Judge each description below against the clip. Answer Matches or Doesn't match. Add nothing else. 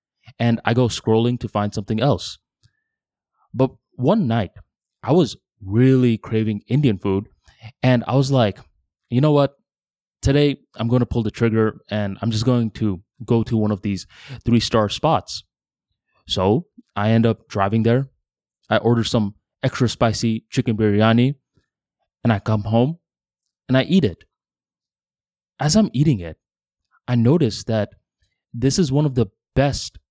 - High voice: Doesn't match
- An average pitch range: Matches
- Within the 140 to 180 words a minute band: Matches